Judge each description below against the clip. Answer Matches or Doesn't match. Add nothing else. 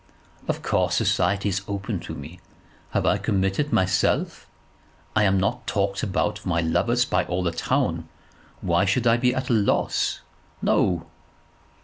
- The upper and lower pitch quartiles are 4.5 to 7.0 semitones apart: Doesn't match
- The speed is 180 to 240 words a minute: Doesn't match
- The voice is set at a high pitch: Doesn't match